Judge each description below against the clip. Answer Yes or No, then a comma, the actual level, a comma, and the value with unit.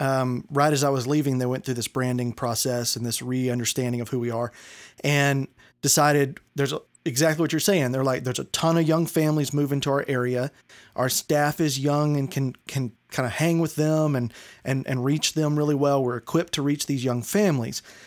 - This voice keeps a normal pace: No, fast, 215 wpm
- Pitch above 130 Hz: Yes, medium, 140 Hz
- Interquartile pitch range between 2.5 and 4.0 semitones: Yes, average, 2.9 semitones